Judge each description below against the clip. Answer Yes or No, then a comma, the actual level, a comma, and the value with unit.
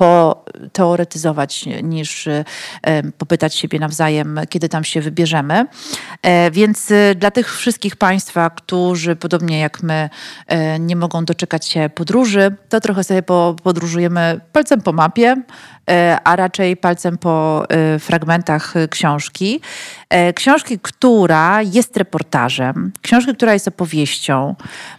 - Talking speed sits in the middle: No, slow, 105 wpm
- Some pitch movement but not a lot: Yes, average, 4.0 semitones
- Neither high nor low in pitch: Yes, medium, 175 Hz